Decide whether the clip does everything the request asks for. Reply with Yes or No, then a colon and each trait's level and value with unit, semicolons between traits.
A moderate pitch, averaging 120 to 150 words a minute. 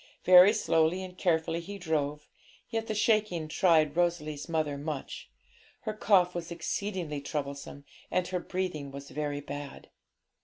Yes: medium, 165 Hz; average, 140 wpm